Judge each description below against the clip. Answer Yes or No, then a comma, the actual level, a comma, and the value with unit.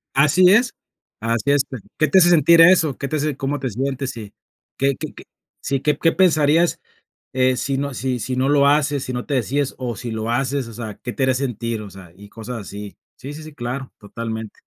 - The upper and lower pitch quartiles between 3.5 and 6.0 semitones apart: Yes, average, 3.8 semitones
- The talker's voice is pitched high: No, low, 135 Hz